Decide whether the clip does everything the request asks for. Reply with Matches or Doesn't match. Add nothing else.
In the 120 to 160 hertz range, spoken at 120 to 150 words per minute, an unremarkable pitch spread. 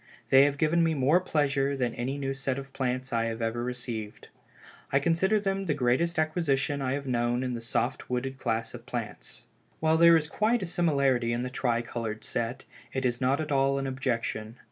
Doesn't match